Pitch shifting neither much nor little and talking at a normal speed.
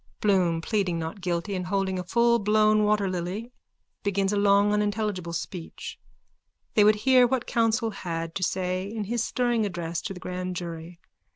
Yes: average, 3.0 semitones; average, 160 wpm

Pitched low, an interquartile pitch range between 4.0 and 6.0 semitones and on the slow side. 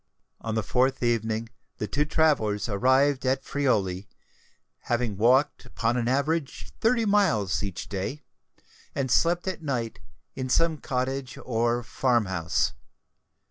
Yes: low, 125 Hz; average, 4.4 semitones; slow, 130 wpm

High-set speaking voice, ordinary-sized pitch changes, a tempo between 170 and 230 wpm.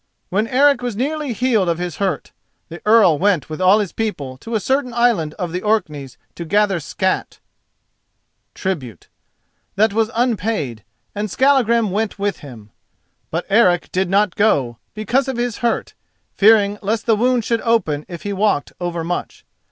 No: high, 205 Hz; average, 4.8 semitones; average, 160 wpm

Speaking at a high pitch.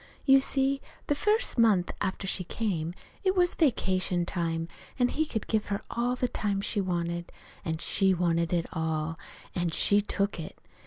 Yes: high, 195 Hz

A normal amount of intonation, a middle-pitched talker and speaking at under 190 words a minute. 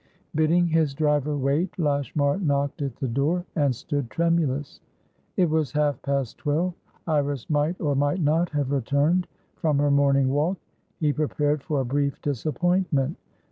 No: narrow, 2.3 semitones; medium, 145 Hz; average, 150 wpm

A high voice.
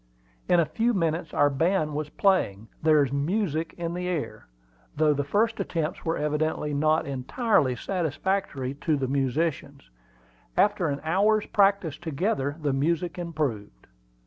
No: medium, 155 Hz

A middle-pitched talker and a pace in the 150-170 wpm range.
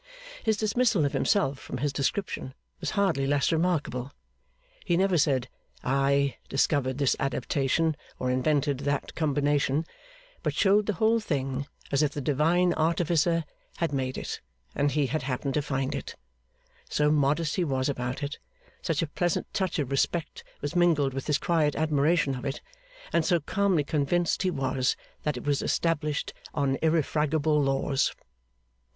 Yes: medium, 145 Hz; average, 155 wpm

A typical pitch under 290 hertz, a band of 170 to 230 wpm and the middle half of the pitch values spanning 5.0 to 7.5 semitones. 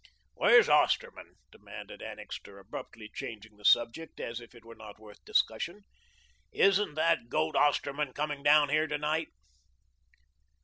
No: medium, 140 Hz; slow, 135 wpm; wide, 5.4 semitones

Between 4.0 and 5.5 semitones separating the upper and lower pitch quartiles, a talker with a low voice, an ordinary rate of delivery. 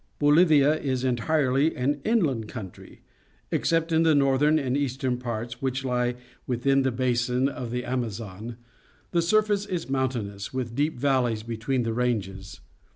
No: average, 3.4 semitones; low, 130 Hz; average, 160 wpm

